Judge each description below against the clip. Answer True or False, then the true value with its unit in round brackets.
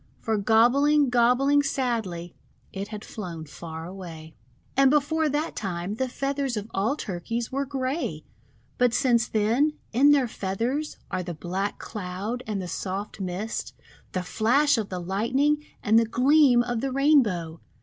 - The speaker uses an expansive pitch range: True (6.2 semitones)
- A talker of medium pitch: False (230 Hz)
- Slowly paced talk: False (160 wpm)